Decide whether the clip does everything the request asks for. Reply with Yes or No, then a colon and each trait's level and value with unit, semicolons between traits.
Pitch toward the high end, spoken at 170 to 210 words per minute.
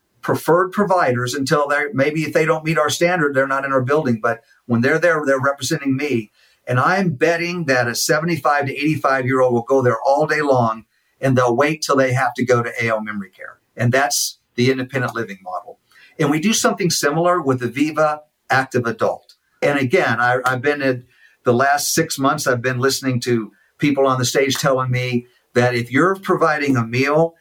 No: low, 135 Hz; fast, 205 wpm